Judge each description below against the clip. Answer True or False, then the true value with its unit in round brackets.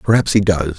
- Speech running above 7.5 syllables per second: False (5.9 syllables/s)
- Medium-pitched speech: False (95 Hz)